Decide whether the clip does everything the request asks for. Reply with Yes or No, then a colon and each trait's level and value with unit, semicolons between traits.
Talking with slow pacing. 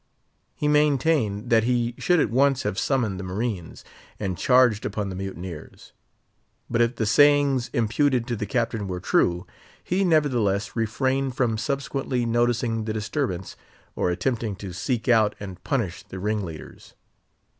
No: average, 145 wpm